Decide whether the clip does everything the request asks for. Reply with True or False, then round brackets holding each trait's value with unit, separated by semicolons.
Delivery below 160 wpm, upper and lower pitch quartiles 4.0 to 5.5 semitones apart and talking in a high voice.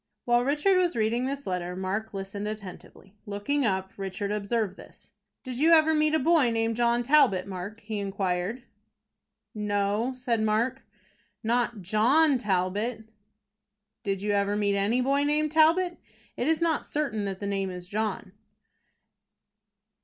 True (150 wpm; 5.0 semitones; 220 Hz)